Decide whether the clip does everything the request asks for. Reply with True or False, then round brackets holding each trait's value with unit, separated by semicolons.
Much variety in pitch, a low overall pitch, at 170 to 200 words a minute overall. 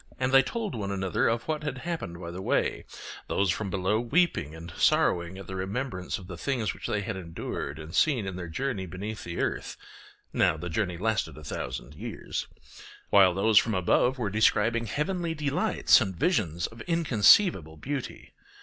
True (6.6 semitones; 100 Hz; 180 wpm)